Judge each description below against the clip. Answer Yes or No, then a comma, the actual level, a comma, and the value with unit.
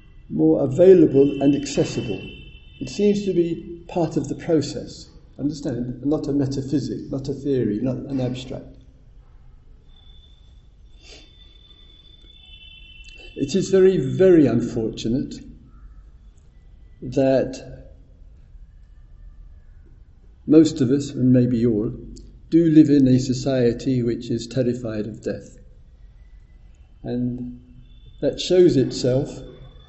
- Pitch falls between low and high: No, low, 125 Hz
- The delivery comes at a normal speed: No, slow, 95 wpm